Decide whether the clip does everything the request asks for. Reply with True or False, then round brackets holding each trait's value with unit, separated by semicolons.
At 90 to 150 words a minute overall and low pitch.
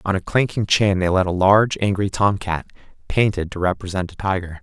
False (205 wpm; 95 Hz)